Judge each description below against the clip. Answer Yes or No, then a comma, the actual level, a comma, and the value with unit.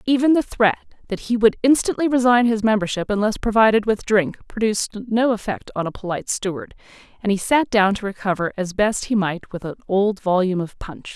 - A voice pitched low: No, high, 210 Hz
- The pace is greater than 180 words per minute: Yes, average, 200 wpm